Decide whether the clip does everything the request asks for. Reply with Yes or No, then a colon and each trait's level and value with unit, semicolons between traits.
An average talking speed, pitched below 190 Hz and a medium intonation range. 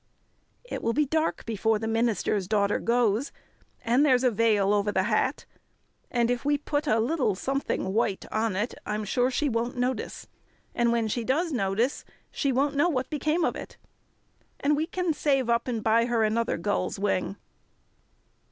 No: average, 175 wpm; high, 235 Hz; average, 4.2 semitones